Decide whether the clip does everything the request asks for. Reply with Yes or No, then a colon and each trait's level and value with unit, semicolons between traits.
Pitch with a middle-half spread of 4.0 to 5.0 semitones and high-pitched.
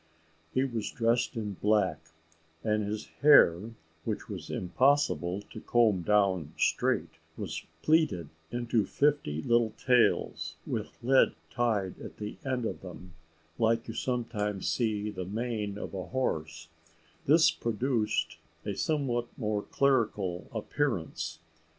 No: average, 4.3 semitones; low, 110 Hz